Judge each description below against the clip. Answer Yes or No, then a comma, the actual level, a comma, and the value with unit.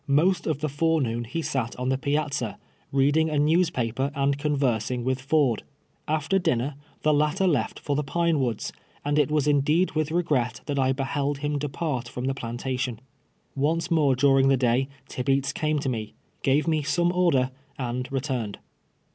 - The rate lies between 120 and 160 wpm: No, average, 175 wpm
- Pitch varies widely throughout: No, average, 3.0 semitones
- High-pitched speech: No, medium, 140 Hz